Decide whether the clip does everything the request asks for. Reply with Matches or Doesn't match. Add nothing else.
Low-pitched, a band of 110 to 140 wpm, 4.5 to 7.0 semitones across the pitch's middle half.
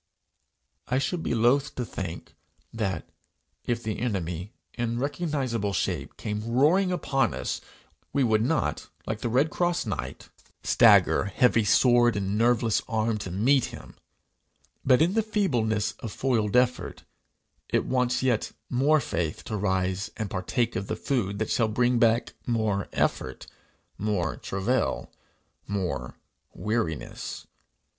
Doesn't match